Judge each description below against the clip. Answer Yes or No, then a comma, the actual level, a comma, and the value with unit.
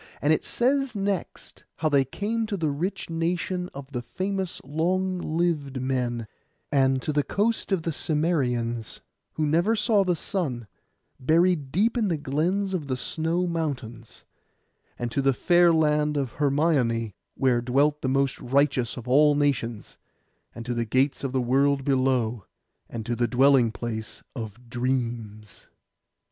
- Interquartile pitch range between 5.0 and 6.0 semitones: Yes, wide, 5.5 semitones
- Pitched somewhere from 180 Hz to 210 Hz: No, medium, 140 Hz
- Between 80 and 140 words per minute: No, average, 155 wpm